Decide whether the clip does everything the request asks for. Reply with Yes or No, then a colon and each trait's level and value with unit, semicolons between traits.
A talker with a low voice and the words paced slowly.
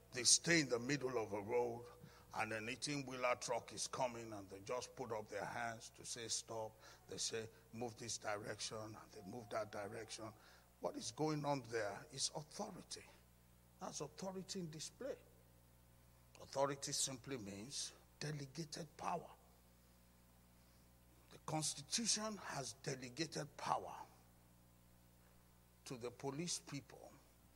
Yes: low, 115 Hz; slow, 130 wpm